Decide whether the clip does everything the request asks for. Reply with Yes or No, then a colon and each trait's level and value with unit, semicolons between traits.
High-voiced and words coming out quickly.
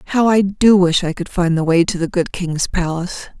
No: medium, 180 Hz; fast, 245 wpm